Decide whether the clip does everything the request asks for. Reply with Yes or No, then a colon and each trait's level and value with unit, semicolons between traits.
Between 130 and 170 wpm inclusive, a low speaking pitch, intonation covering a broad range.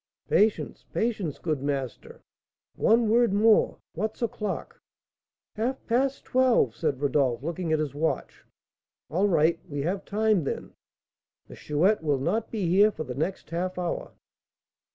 No: average, 140 wpm; medium, 180 Hz; wide, 6.3 semitones